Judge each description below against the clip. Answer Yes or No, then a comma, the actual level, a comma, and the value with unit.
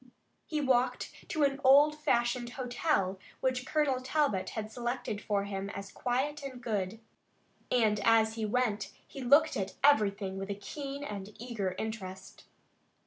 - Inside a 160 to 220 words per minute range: No, average, 145 wpm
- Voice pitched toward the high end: Yes, high, 240 Hz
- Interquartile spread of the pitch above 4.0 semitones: Yes, average, 5.0 semitones